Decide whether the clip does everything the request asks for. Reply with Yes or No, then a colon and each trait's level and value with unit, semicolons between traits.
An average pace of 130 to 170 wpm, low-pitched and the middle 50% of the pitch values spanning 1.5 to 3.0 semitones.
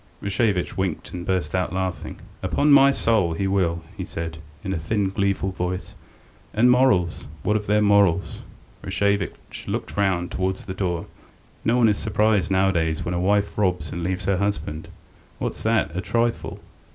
Yes: average, 165 wpm; very low, 95 Hz; average, 2.7 semitones